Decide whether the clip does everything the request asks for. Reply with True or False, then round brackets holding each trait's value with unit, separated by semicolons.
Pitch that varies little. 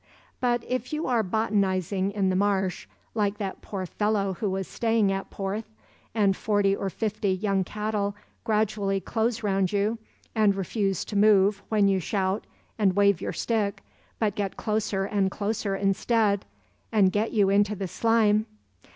True (1.9 semitones)